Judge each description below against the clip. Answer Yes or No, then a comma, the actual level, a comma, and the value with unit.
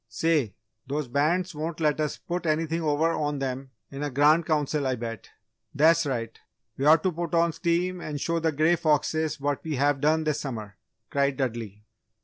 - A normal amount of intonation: Yes, average, 3.0 semitones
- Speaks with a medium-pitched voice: Yes, medium, 150 Hz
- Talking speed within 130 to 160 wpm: No, average, 185 wpm